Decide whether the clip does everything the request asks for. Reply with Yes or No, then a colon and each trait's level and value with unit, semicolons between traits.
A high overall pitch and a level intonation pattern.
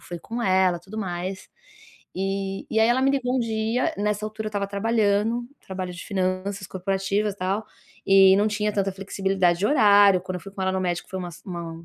Yes: high, 195 Hz; narrow, 2.3 semitones